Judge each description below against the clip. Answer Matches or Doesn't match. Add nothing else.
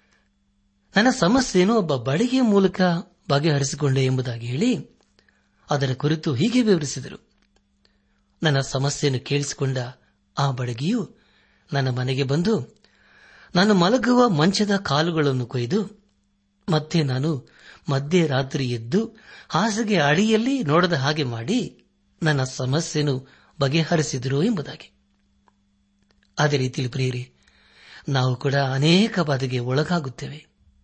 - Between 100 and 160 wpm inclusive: Doesn't match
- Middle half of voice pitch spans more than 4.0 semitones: Matches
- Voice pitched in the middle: Matches